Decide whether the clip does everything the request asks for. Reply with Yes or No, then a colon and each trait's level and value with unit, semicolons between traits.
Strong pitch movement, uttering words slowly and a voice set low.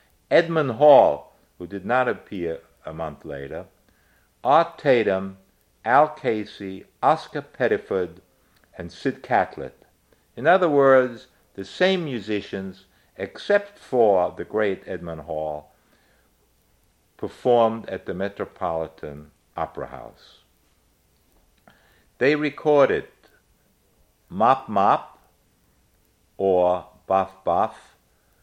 Yes: wide, 6.7 semitones; slow, 90 wpm; very low, 95 Hz